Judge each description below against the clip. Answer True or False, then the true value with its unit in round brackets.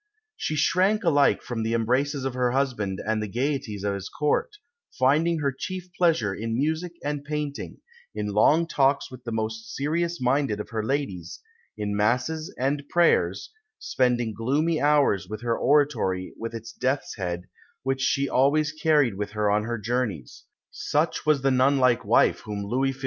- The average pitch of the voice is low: True (130 Hz)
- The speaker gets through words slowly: False (170 wpm)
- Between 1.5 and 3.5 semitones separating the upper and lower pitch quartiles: False (5.0 semitones)